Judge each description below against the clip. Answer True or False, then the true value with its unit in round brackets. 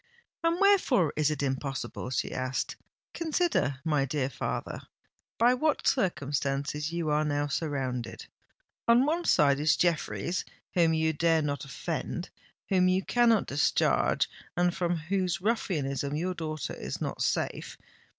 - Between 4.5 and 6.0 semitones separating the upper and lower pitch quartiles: True (4.8 semitones)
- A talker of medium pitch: True (155 Hz)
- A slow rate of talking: True (130 wpm)